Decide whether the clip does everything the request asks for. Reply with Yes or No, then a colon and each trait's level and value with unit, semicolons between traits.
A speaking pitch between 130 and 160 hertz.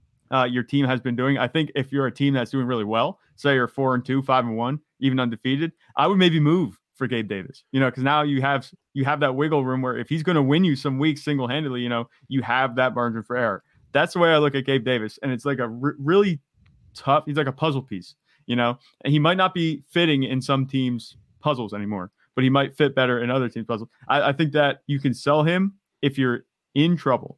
Yes: low, 135 Hz